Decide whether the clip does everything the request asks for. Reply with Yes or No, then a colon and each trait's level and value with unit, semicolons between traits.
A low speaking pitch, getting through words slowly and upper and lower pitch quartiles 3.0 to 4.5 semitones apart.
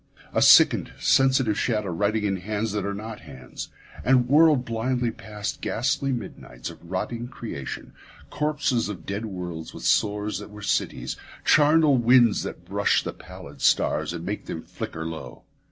No: low, 110 Hz; average, 155 wpm; average, 4.2 semitones